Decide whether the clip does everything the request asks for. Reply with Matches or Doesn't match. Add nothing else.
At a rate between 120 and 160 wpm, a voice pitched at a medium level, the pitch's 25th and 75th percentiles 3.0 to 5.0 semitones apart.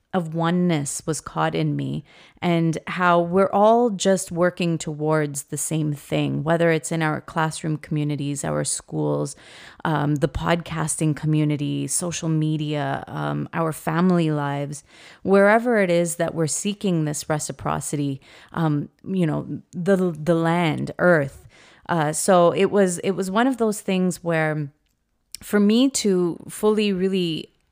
Matches